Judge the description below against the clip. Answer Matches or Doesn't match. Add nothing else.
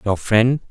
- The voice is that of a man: Matches